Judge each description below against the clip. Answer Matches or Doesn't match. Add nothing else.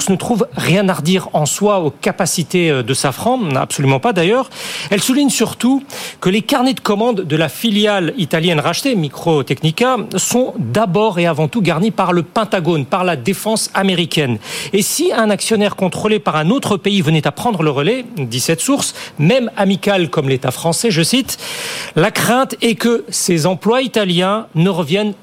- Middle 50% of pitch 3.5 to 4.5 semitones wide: Doesn't match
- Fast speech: Doesn't match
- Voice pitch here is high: Matches